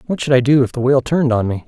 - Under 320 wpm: No, fast, 360 wpm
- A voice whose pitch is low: Yes, low, 130 Hz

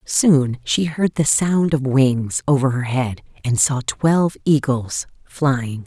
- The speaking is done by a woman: Yes, female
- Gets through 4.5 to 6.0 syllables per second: No, 3.5 syllables/s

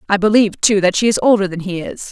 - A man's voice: No, female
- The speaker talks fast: Yes, fast, 285 wpm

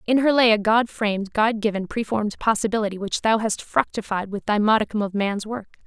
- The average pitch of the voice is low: No, high, 215 Hz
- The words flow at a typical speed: Yes, average, 185 wpm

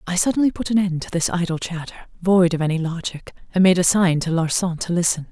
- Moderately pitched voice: Yes, medium, 175 Hz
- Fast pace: Yes, fast, 225 wpm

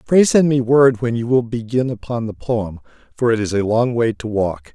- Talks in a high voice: No, low, 120 Hz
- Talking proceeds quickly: Yes, fast, 240 wpm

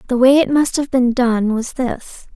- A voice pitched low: No, very high, 250 Hz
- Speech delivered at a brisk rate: Yes, fast, 230 wpm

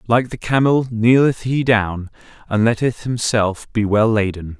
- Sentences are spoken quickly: No, average, 155 wpm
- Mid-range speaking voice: No, low, 115 Hz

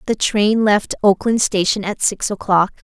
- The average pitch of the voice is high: Yes, high, 205 Hz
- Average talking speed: Yes, average, 165 wpm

